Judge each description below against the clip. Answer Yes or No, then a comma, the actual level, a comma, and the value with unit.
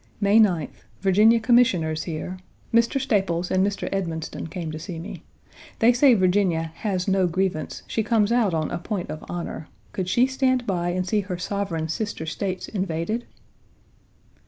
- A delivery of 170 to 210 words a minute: No, average, 160 wpm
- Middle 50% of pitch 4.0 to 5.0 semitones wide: Yes, average, 4.3 semitones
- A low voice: No, high, 190 Hz